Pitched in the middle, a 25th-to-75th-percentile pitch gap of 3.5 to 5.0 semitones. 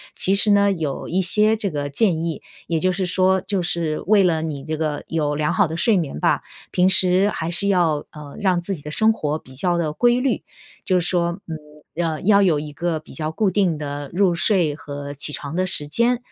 Yes: medium, 170 Hz; average, 3.9 semitones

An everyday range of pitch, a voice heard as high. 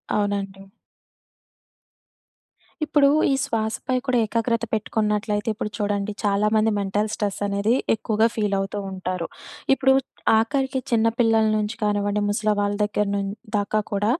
No: narrow, 1.7 semitones; high, 210 Hz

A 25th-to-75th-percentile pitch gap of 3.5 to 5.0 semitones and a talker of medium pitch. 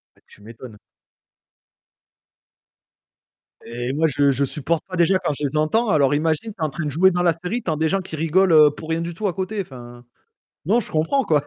Yes: average, 4.1 semitones; medium, 160 Hz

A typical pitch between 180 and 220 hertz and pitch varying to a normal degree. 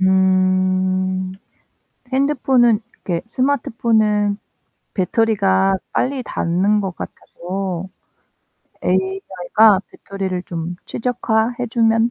Yes: high, 195 Hz; average, 3.2 semitones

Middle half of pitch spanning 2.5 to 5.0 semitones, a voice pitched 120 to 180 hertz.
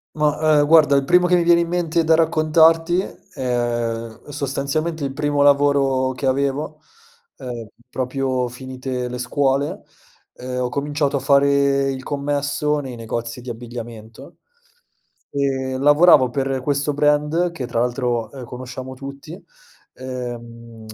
Yes: average, 2.8 semitones; low, 135 Hz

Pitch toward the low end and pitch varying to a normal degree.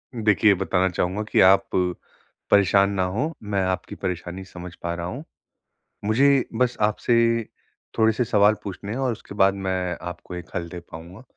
Yes: low, 100 Hz; average, 3.4 semitones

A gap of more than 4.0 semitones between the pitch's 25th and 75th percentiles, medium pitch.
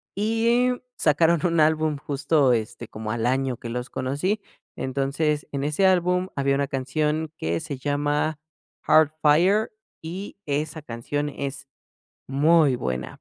No: average, 3.2 semitones; medium, 145 Hz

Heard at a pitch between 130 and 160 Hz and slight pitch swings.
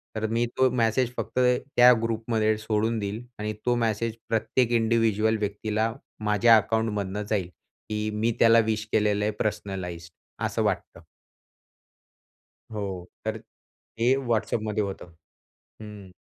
No: low, 110 Hz; narrow, 1.7 semitones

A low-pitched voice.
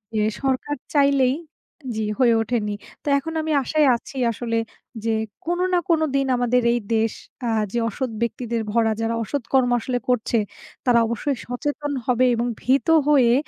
No: very high, 250 Hz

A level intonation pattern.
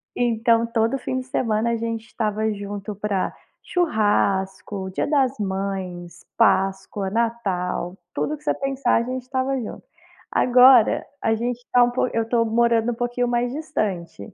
No: average, 3.6 semitones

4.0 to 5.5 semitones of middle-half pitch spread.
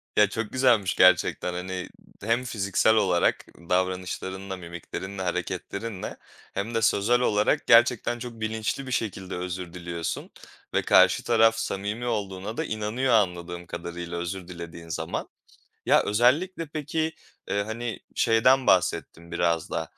Yes: average, 4.3 semitones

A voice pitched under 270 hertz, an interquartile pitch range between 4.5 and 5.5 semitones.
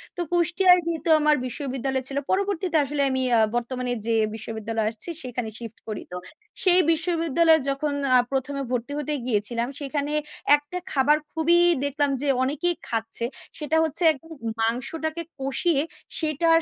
No: very high, 285 Hz; average, 4.8 semitones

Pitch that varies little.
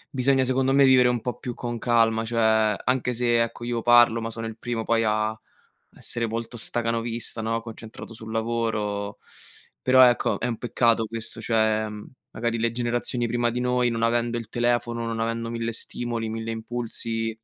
Yes: narrow, 1.2 semitones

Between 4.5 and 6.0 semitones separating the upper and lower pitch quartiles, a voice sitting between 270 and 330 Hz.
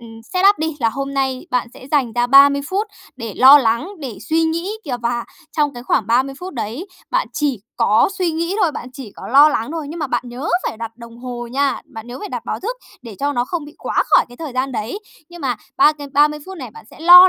Yes: average, 4.9 semitones; very high, 275 Hz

